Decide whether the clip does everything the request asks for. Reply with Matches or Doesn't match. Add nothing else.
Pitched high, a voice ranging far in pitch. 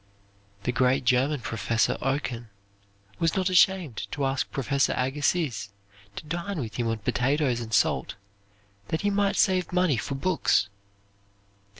Doesn't match